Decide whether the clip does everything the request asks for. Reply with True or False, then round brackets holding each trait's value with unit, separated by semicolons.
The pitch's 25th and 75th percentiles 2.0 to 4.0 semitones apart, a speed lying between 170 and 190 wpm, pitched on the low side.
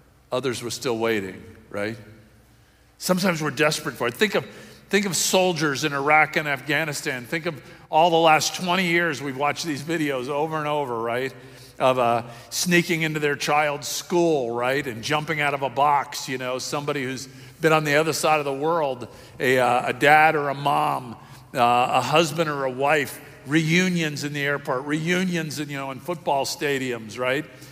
False (3.5 semitones; 185 wpm; 145 Hz)